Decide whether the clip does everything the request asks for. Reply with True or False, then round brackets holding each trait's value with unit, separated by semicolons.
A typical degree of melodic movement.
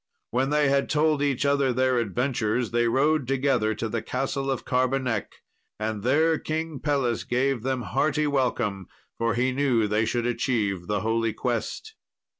True (3.5 semitones)